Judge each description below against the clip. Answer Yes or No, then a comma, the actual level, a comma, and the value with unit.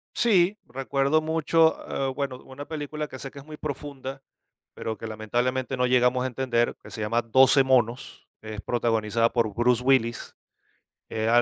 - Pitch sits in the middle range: No, low, 130 Hz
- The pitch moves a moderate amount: Yes, average, 3.2 semitones